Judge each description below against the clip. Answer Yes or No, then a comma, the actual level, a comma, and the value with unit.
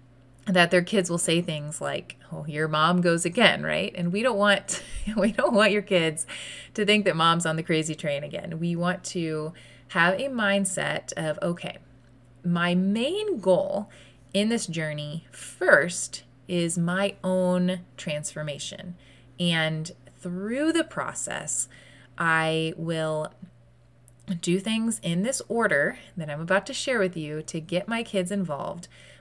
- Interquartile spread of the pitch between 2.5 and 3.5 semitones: No, average, 4.1 semitones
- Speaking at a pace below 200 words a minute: Yes, average, 150 wpm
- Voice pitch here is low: No, medium, 175 Hz